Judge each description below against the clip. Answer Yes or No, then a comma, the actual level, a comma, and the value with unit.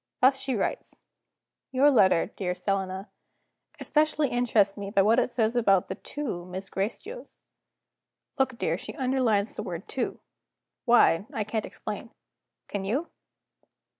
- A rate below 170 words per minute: Yes, average, 140 wpm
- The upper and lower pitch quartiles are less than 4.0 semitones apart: No, average, 4.8 semitones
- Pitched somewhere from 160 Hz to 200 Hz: No, high, 220 Hz